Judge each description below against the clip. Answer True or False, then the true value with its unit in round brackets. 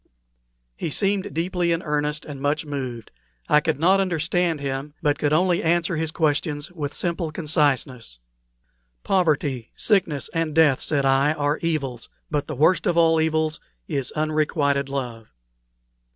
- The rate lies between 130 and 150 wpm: True (145 wpm)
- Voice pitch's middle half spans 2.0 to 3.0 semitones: True (2.6 semitones)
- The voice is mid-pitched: True (150 Hz)